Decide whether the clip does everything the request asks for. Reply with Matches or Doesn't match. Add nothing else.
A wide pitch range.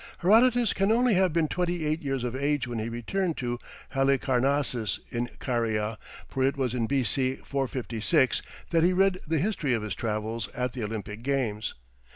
Matches